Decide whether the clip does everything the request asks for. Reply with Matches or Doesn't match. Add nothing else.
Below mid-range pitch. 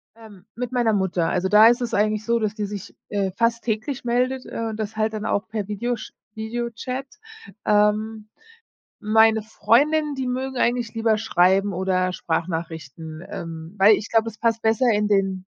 Doesn't match